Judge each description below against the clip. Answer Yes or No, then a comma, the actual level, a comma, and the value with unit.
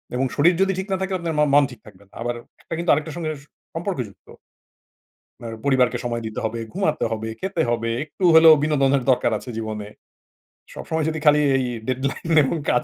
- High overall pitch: No, medium, 140 Hz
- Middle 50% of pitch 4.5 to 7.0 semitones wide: Yes, average, 5.3 semitones